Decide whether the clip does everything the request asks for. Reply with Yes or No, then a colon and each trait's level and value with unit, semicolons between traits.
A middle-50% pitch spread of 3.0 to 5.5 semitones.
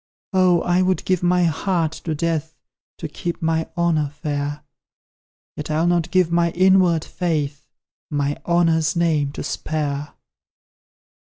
No: narrow, 2.6 semitones